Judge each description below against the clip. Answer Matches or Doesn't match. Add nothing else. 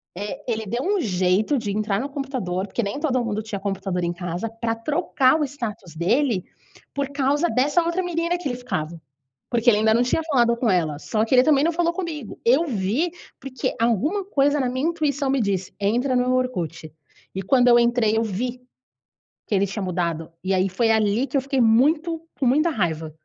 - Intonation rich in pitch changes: Matches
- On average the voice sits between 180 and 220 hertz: Doesn't match